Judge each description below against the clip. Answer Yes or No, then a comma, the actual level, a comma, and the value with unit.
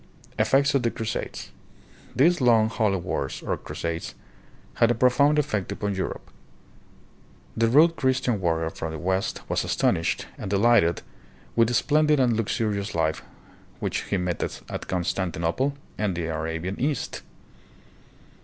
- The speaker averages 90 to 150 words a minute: Yes, slow, 135 wpm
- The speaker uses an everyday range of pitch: No, wide, 6.6 semitones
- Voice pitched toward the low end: Yes, low, 110 Hz